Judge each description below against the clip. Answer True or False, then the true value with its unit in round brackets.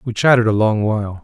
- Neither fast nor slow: False (245 wpm)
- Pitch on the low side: True (110 Hz)